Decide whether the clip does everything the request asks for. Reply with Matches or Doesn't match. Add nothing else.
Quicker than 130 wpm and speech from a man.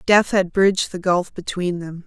Doesn't match